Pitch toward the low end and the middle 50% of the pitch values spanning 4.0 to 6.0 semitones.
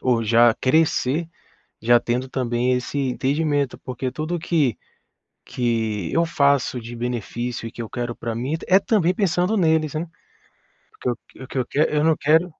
Yes: low, 130 Hz; average, 4.9 semitones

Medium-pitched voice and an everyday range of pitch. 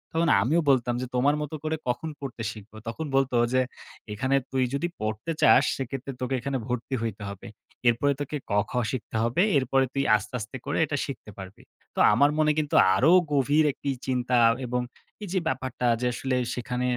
No: low, 130 Hz; average, 3.0 semitones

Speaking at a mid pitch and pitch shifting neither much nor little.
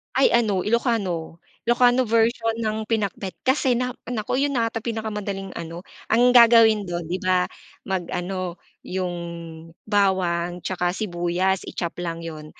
No: high, 200 Hz; average, 4.5 semitones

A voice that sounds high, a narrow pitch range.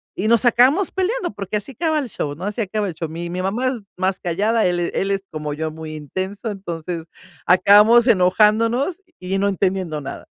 No: high, 195 Hz; average, 4.7 semitones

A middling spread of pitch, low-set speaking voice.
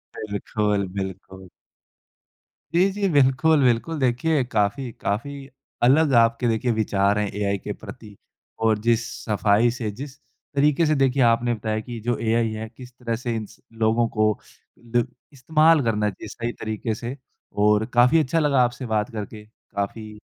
Yes: average, 3.5 semitones; low, 115 Hz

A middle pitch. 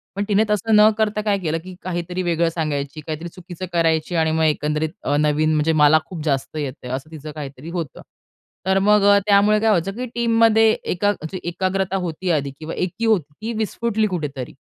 Yes: medium, 175 Hz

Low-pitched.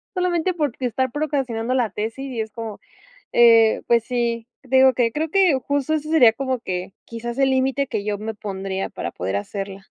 No: high, 240 Hz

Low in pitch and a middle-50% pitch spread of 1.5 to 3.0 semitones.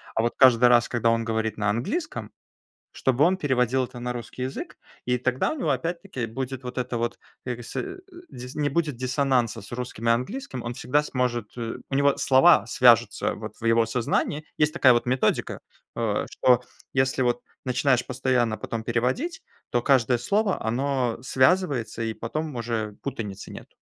Yes: low, 125 Hz; average, 2.7 semitones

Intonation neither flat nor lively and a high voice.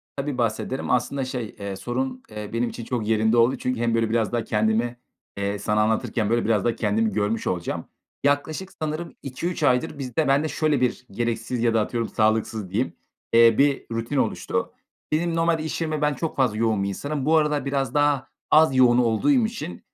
No: average, 4.4 semitones; low, 120 Hz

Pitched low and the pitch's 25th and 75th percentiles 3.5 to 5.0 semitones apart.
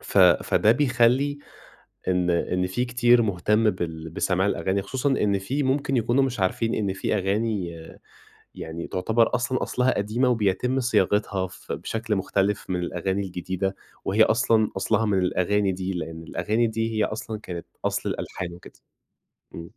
Yes: low, 105 Hz; average, 4.2 semitones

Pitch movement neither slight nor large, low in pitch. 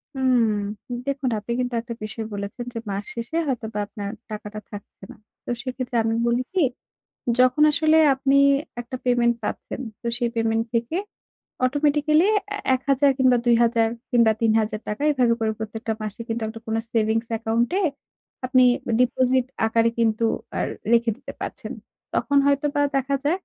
No: average, 3.0 semitones; high, 240 Hz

